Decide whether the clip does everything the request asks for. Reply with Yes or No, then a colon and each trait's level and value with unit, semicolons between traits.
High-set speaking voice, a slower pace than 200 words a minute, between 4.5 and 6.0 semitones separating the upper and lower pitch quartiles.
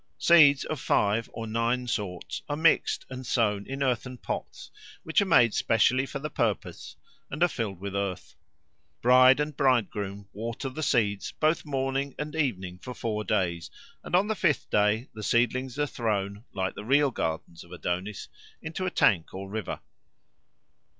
No: low, 120 Hz; average, 165 wpm; wide, 5.4 semitones